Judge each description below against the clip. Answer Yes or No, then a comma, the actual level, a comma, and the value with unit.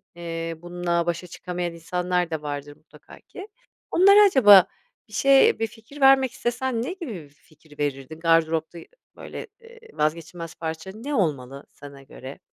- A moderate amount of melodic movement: No, wide, 6.4 semitones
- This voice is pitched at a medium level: Yes, medium, 170 Hz